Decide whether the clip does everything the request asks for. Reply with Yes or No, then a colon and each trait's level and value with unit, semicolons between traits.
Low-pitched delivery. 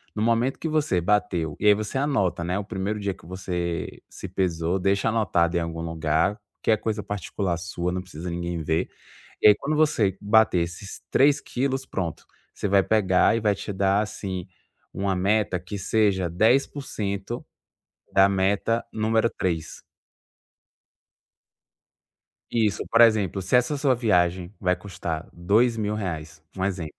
Yes: low, 100 Hz